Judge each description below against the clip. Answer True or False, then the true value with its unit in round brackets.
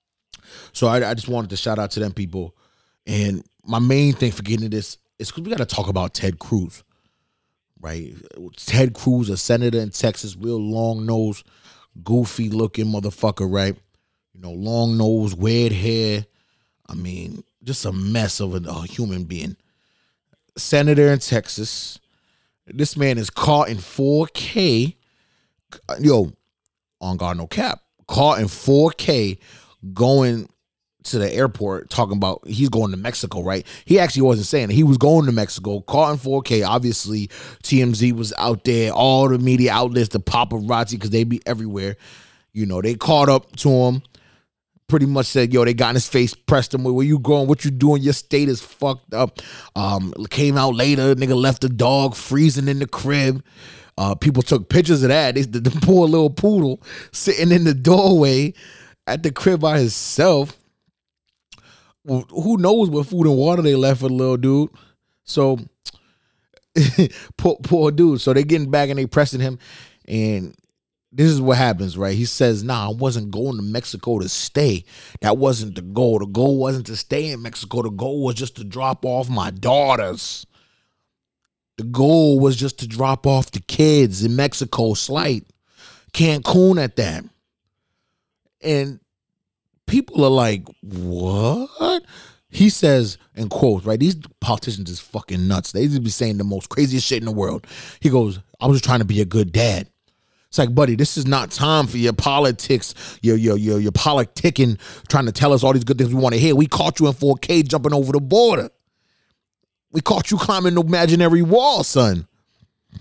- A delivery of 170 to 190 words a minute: True (175 wpm)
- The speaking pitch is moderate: False (125 Hz)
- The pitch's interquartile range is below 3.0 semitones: False (4.7 semitones)